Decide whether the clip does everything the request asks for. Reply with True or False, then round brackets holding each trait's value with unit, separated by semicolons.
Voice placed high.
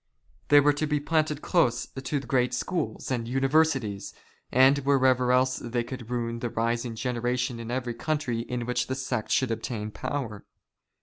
False (125 Hz)